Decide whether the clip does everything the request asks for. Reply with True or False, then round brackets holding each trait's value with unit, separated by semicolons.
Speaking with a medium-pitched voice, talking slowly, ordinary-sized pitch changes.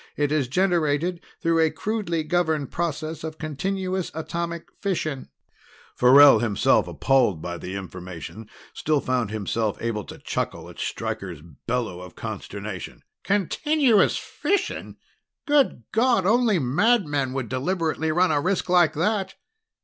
False (155 Hz; 125 wpm; 7.1 semitones)